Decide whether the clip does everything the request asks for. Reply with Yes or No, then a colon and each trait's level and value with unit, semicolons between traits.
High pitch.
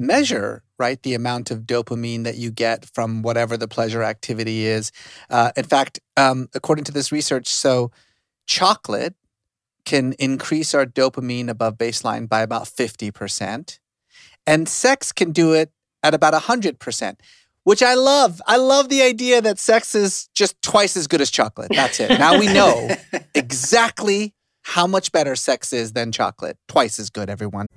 No: low, 130 Hz